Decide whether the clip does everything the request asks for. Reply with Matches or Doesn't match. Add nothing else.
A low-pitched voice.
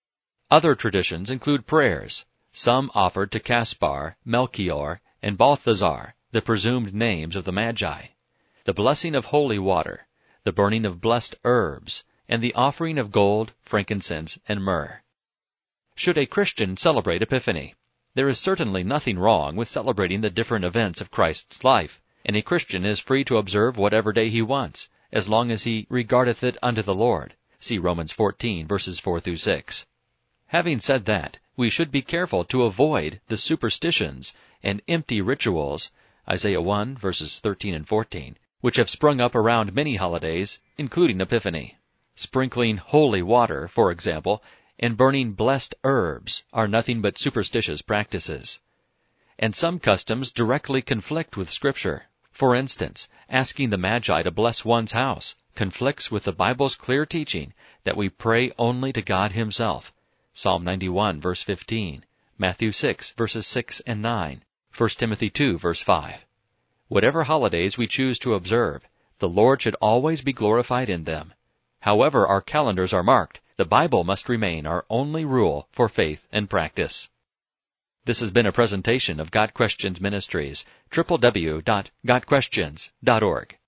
Matches